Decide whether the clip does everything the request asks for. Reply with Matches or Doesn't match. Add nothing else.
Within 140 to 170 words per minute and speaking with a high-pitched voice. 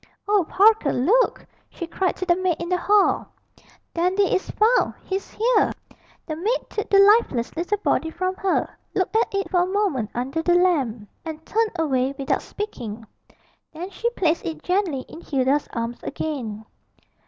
Matches